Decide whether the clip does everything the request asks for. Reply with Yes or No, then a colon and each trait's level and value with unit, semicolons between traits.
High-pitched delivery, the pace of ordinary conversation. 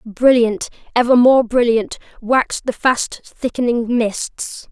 No: high, 240 Hz; slow, 115 wpm